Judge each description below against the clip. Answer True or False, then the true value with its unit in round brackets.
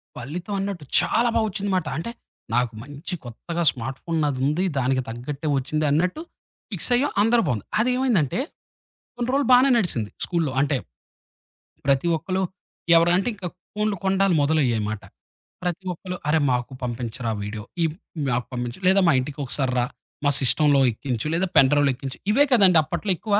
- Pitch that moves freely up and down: True (6.6 semitones)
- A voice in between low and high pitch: True (155 Hz)